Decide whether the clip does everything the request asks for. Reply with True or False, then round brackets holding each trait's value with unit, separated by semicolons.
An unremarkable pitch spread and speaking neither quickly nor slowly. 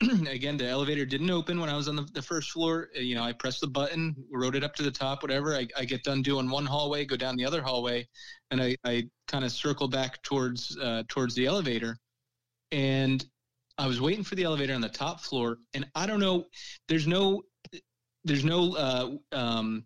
False (3.8 semitones; 215 wpm)